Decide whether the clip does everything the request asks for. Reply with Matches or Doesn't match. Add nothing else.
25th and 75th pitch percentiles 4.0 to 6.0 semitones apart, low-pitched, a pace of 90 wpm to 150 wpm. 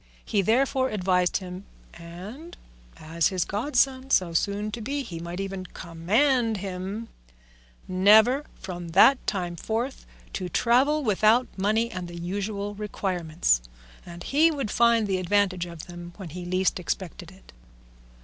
Doesn't match